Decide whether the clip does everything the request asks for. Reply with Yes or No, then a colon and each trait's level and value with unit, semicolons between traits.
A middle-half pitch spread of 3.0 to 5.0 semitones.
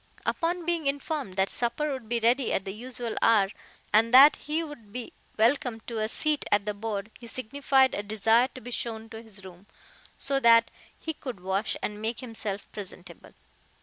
Yes: average, 4.2 semitones